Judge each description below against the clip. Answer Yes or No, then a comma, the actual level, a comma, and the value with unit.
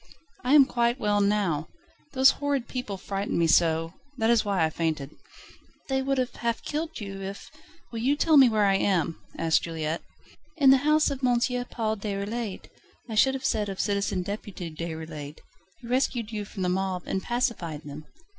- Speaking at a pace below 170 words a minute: No, average, 185 wpm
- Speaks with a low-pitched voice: No, high, 205 Hz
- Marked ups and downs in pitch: Yes, wide, 6.3 semitones